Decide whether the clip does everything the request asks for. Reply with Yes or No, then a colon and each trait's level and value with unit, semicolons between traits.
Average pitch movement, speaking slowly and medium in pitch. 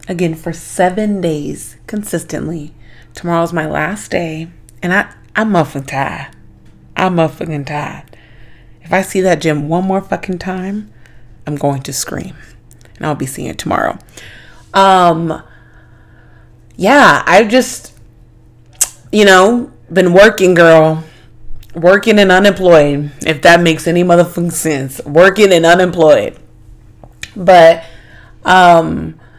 No: wide, 7.1 semitones; slow, 120 wpm; medium, 160 Hz